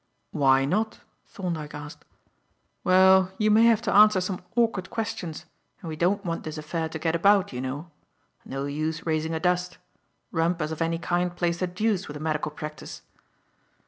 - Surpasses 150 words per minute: Yes, average, 175 wpm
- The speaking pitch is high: No, medium, 170 Hz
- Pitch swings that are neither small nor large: Yes, average, 3.5 semitones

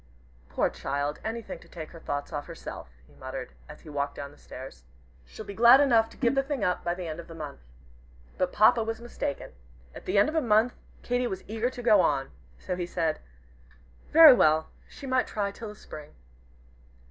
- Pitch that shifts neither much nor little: No, wide, 7.3 semitones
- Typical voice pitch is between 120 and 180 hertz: No, high, 200 Hz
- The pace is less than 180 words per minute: No, fast, 205 wpm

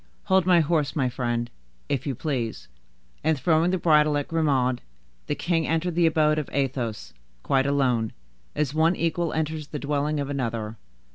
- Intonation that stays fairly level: No, average, 3.5 semitones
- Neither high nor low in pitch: Yes, medium, 150 Hz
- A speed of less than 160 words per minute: No, average, 165 wpm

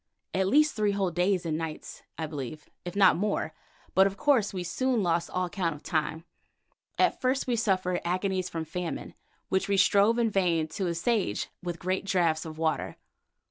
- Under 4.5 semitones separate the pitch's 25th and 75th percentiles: Yes, average, 3.3 semitones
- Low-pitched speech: No, medium, 185 Hz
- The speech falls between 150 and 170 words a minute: No, average, 180 wpm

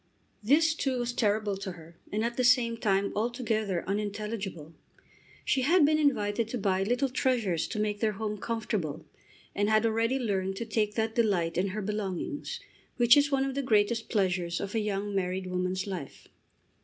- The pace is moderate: Yes, average, 180 wpm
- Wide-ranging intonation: No, average, 3.7 semitones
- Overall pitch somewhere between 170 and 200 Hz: No, high, 210 Hz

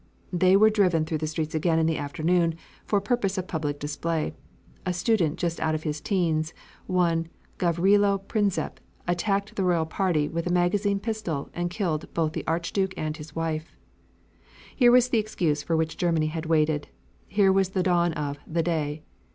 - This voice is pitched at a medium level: Yes, medium, 170 Hz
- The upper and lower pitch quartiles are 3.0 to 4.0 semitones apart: Yes, average, 3.4 semitones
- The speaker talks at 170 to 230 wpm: Yes, average, 175 wpm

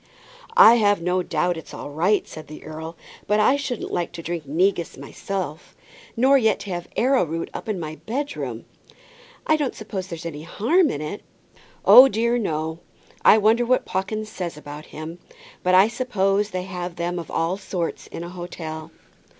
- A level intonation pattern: No, average, 4.7 semitones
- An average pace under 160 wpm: No, average, 175 wpm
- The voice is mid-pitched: Yes, medium, 180 Hz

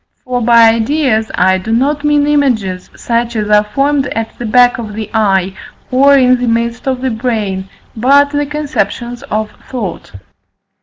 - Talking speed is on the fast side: No, average, 165 wpm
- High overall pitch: Yes, high, 235 Hz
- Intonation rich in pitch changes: No, average, 3.8 semitones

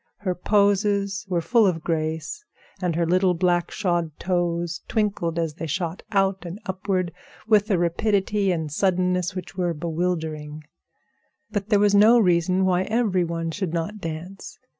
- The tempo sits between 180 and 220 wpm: No, average, 155 wpm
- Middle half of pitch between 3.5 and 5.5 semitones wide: No, average, 3.0 semitones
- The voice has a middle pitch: Yes, medium, 180 Hz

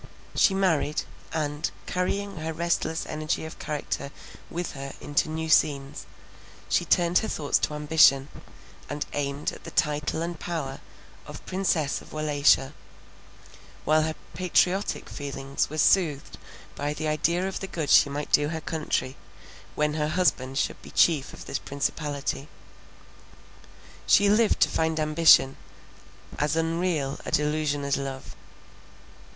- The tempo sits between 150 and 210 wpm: No, average, 140 wpm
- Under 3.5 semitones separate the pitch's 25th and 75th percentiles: Yes, narrow, 2.5 semitones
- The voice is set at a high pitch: No, medium, 155 Hz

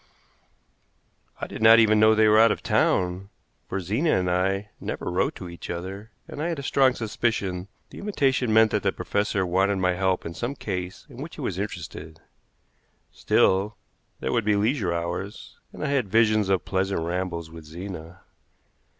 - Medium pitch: No, low, 100 Hz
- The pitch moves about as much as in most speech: Yes, average, 3.6 semitones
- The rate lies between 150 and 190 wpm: Yes, average, 180 wpm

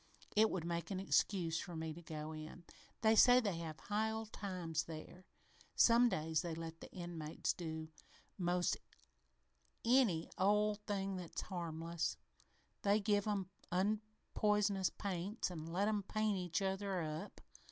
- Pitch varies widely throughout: No, average, 4.0 semitones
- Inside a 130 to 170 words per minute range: Yes, average, 150 wpm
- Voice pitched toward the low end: No, medium, 185 Hz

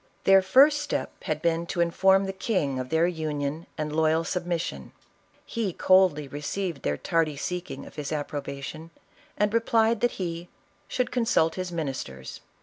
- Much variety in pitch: No, average, 4.4 semitones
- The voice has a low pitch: No, medium, 165 Hz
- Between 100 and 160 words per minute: Yes, average, 150 wpm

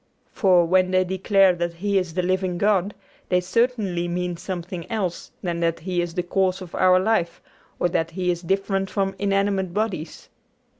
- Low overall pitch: No, medium, 185 Hz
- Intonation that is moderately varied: No, narrow, 2.0 semitones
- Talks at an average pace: Yes, average, 180 wpm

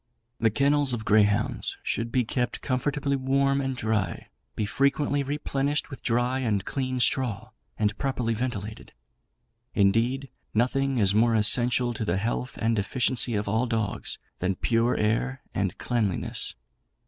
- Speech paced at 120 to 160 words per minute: Yes, average, 140 wpm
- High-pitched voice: No, low, 120 Hz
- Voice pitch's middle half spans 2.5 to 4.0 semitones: Yes, average, 3.6 semitones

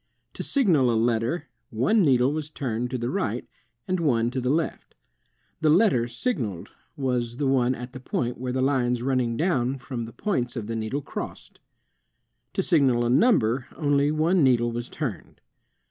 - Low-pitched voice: Yes, low, 130 Hz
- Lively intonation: No, average, 3.7 semitones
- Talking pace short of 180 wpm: Yes, average, 170 wpm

